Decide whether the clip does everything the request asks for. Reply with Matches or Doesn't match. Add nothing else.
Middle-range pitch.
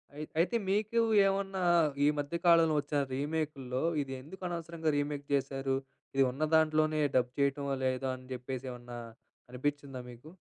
Matches